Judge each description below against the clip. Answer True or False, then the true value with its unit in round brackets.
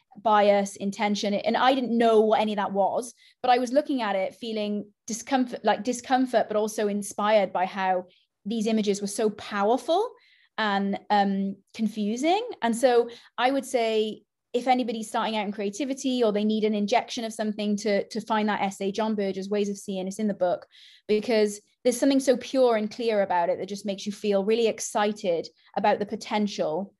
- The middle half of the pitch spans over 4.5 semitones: False (3.0 semitones)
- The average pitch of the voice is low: False (215 Hz)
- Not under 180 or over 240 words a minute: True (185 wpm)